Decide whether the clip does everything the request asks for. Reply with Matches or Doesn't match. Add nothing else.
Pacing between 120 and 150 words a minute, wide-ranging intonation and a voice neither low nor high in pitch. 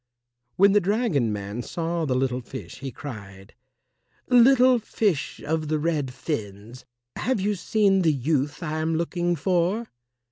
Matches